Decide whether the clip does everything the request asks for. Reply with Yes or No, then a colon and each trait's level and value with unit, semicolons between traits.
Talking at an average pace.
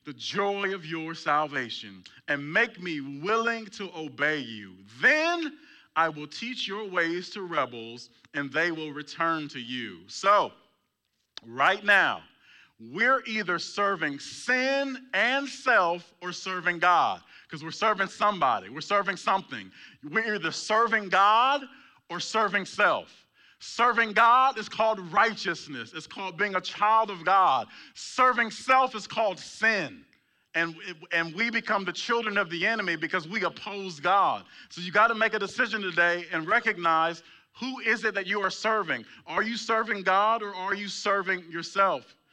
Yes: average, 155 wpm